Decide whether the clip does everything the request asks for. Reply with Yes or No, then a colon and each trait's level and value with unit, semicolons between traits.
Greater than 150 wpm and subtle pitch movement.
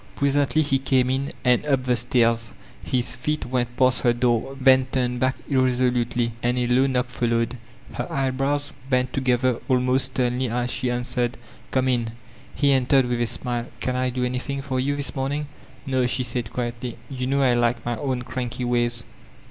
Yes: average, 180 wpm; narrow, 1.4 semitones